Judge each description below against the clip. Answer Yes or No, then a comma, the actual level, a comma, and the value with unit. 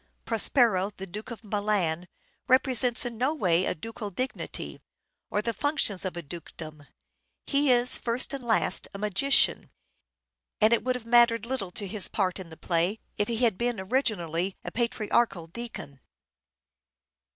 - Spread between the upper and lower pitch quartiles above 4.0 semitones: Yes, average, 4.6 semitones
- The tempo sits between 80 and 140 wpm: No, average, 155 wpm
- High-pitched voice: Yes, high, 215 Hz